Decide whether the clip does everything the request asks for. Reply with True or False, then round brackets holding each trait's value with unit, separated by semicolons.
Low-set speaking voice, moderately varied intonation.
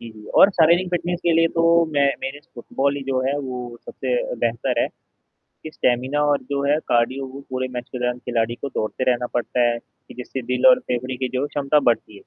True (130 Hz; 3.0 semitones)